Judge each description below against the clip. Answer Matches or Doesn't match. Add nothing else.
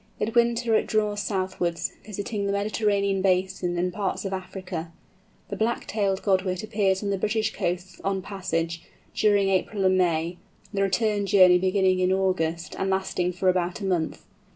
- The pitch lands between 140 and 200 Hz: Matches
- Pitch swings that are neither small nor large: Doesn't match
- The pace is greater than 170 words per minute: Doesn't match